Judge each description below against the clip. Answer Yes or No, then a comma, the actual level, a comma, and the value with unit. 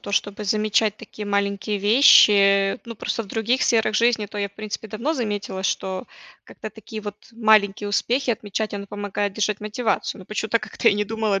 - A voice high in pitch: Yes, high, 210 Hz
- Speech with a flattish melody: Yes, narrow, 1.6 semitones